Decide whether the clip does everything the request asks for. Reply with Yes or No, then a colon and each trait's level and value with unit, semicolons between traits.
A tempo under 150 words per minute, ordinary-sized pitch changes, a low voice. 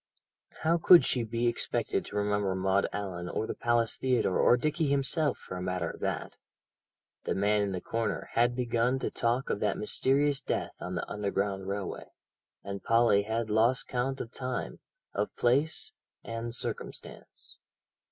No: average, 160 wpm; average, 4.1 semitones; low, 115 Hz